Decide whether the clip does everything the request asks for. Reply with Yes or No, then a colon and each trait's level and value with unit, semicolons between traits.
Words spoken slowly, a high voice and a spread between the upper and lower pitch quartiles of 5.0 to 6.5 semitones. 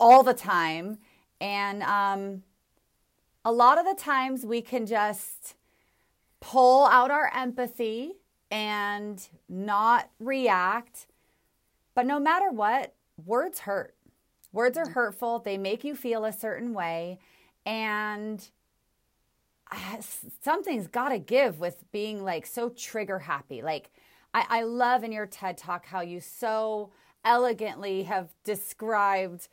No: slow, 125 wpm; high, 220 Hz; average, 3.7 semitones